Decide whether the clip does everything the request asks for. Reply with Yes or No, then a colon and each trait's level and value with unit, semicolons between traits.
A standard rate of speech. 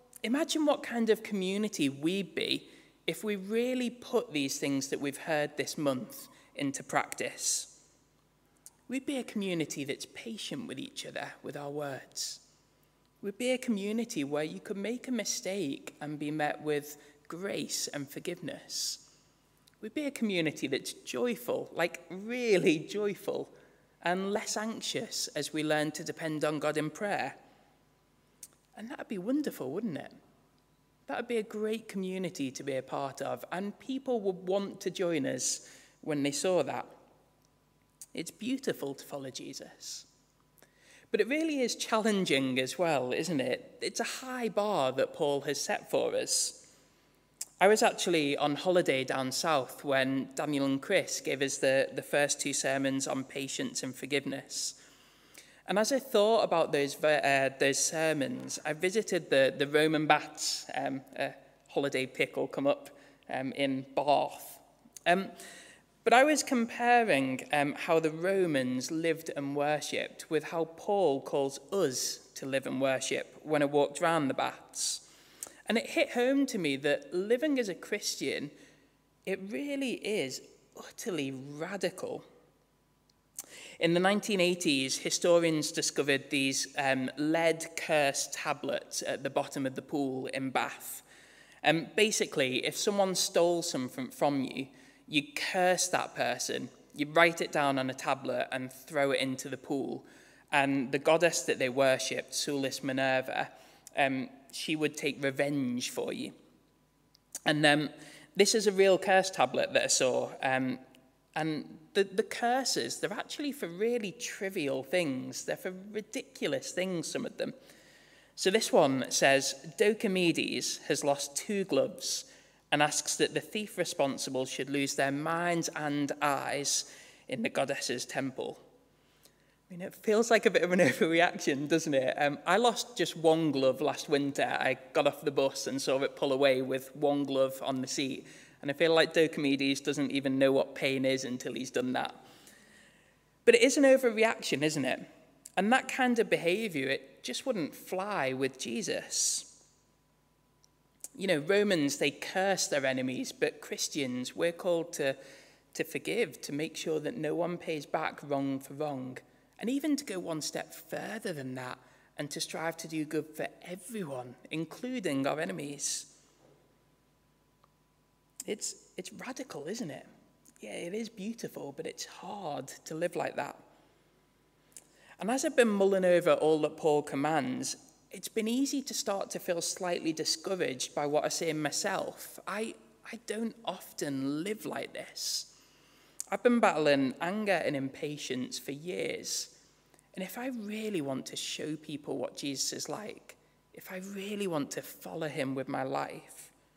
Yes: average, 160 wpm